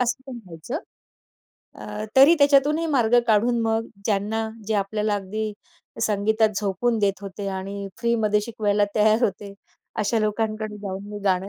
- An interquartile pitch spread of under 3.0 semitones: Yes, narrow, 2.5 semitones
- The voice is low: No, high, 215 Hz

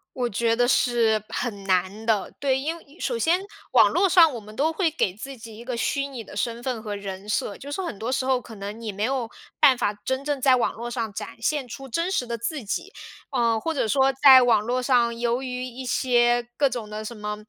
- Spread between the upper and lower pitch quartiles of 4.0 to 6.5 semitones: No, average, 3.5 semitones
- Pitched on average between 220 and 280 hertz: Yes, high, 240 Hz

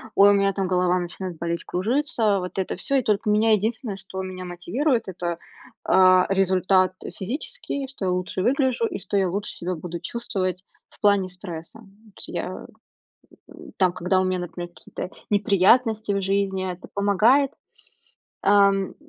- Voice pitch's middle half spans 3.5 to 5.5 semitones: No, narrow, 2.6 semitones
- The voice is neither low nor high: No, high, 195 Hz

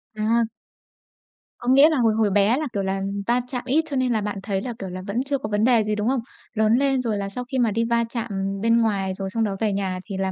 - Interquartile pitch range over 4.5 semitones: No, average, 3.6 semitones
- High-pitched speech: Yes, high, 220 Hz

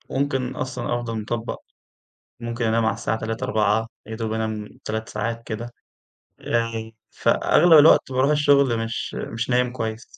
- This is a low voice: Yes, low, 115 Hz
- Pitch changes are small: Yes, narrow, 2.2 semitones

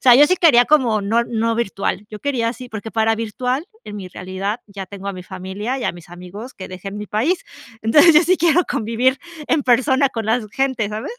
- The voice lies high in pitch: Yes, high, 225 Hz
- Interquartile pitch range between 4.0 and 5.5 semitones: Yes, average, 4.5 semitones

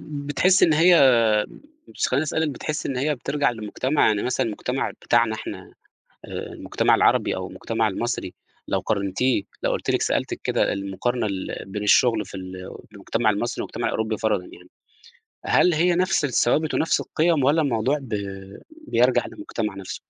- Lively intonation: Yes, wide, 6.1 semitones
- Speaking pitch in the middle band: No, low, 120 Hz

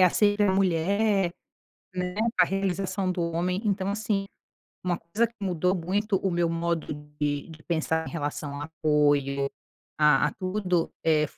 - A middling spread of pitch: Yes, average, 3.5 semitones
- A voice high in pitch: No, medium, 175 Hz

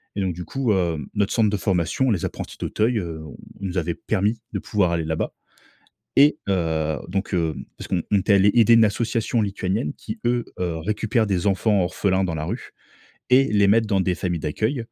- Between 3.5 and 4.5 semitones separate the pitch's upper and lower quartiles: Yes, average, 4.0 semitones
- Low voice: Yes, low, 100 Hz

